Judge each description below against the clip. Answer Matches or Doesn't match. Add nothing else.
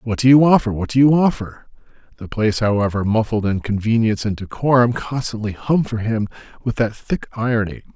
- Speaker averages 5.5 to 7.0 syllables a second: Matches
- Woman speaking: Doesn't match